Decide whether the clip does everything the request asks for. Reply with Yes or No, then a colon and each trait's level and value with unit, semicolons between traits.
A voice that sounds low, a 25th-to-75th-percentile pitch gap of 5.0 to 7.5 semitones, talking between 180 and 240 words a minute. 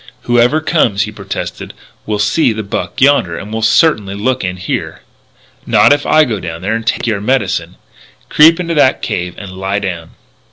Yes: low, 110 Hz; wide, 5.5 semitones; average, 190 wpm